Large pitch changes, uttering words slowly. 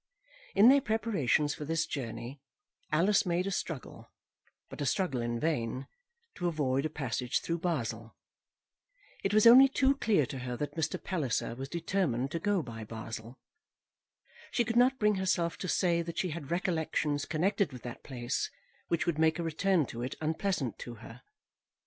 No: wide, 6.6 semitones; average, 170 wpm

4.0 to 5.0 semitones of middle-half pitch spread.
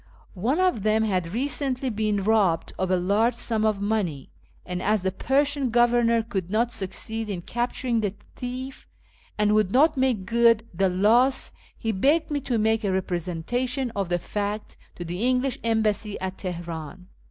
Yes: average, 4.3 semitones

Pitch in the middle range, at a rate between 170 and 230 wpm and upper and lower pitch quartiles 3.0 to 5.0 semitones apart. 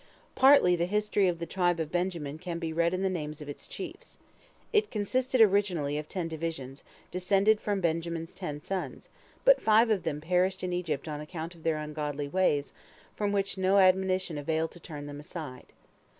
Yes: medium, 175 Hz; average, 185 wpm; average, 3.9 semitones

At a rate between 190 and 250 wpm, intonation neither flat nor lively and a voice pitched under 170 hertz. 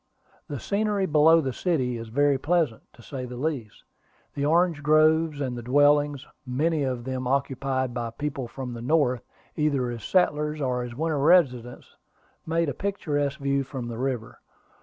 No: average, 165 wpm; average, 3.7 semitones; medium, 140 Hz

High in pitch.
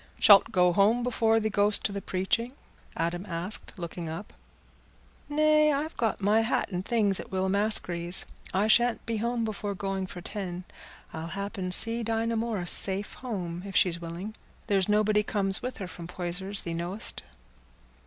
Yes: high, 200 Hz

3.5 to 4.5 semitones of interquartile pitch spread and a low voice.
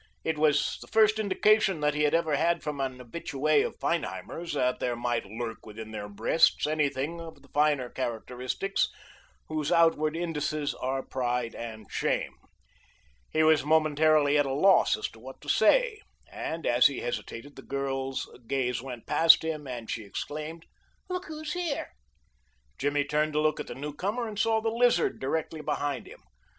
No: average, 4.2 semitones; medium, 150 Hz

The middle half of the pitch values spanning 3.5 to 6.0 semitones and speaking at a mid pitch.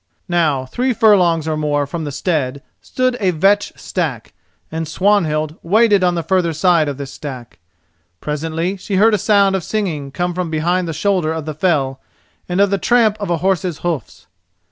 Yes: average, 4.2 semitones; medium, 170 Hz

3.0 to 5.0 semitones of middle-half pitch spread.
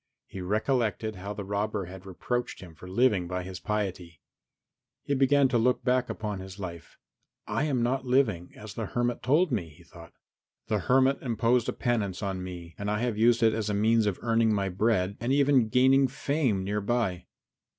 Yes: average, 4.6 semitones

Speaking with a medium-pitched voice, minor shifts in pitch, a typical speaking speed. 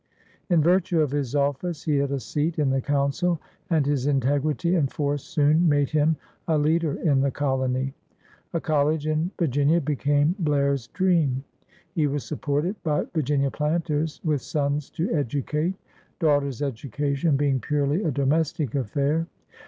Yes: medium, 145 Hz; narrow, 2.2 semitones; average, 160 wpm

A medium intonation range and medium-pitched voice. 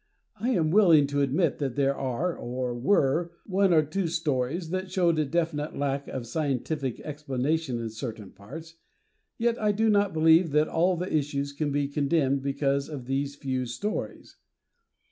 Yes: average, 3.7 semitones; medium, 150 Hz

